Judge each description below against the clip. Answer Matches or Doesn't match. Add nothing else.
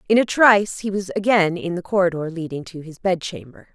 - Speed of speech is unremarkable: Doesn't match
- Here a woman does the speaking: Matches